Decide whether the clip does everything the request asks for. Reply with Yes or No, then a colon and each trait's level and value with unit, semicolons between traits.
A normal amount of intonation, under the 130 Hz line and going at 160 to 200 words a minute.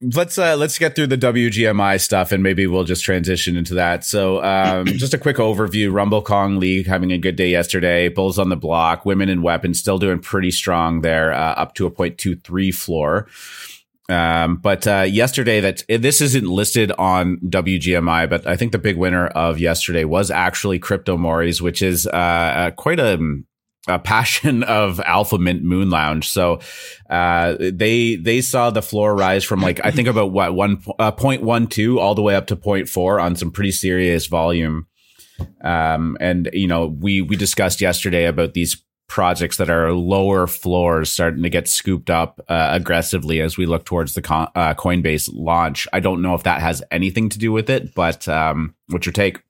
Yes: average, 3.0 semitones; very low, 95 Hz; average, 190 wpm